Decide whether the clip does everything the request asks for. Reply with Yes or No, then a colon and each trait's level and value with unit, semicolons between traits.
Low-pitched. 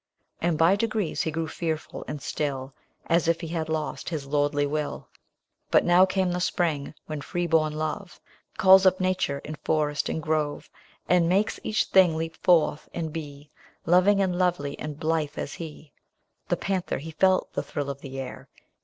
No: medium, 160 Hz